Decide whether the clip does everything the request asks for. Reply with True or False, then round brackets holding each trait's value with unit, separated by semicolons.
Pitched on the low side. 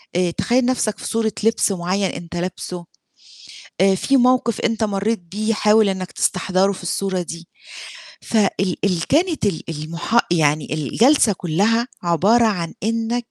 False (195 Hz)